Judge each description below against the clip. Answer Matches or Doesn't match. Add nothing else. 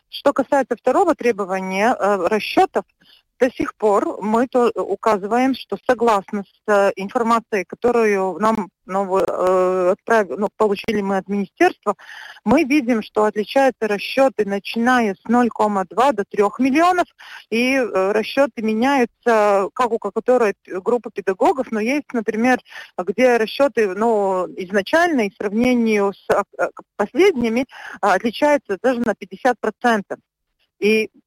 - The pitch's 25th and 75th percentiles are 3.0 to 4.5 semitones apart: Matches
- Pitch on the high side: Matches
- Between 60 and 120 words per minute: Matches